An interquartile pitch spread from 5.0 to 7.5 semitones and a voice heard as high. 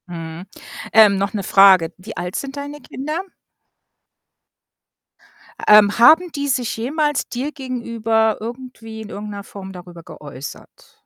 Yes: wide, 5.4 semitones; high, 220 Hz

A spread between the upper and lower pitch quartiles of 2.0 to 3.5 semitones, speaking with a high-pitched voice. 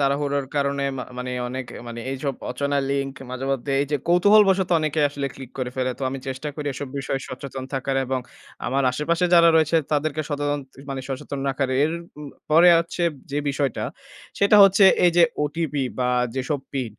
No: narrow, 2.6 semitones; medium, 140 Hz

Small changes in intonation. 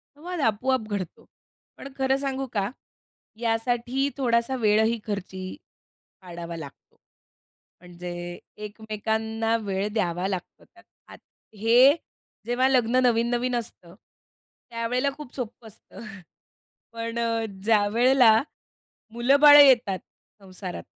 No: average, 3.7 semitones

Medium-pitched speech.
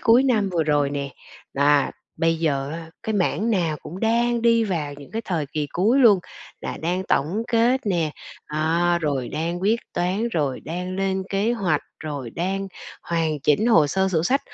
Yes: medium, 175 Hz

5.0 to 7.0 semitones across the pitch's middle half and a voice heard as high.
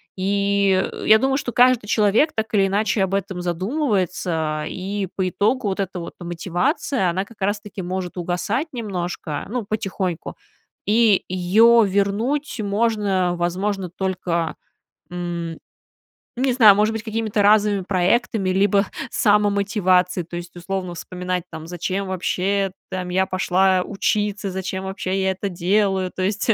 No: narrow, 2.4 semitones; high, 195 Hz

